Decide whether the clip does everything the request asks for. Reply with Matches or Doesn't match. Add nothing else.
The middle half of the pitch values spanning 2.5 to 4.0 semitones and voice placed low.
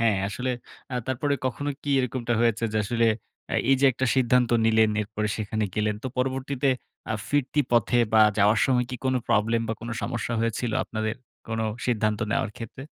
Matches